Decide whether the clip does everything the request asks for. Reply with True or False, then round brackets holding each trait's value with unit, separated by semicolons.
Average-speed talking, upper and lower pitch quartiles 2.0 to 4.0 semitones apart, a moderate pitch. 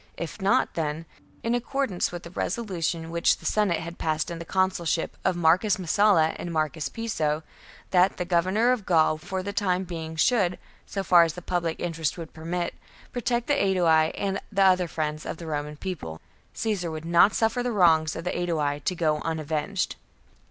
True (190 wpm; 3.3 semitones; 175 Hz)